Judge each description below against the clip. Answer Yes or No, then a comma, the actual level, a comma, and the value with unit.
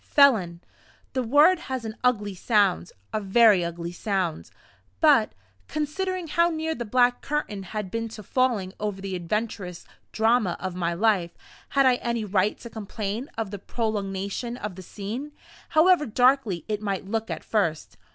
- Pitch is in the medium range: No, high, 215 Hz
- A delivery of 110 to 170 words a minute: Yes, average, 160 wpm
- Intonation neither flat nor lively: Yes, average, 4.6 semitones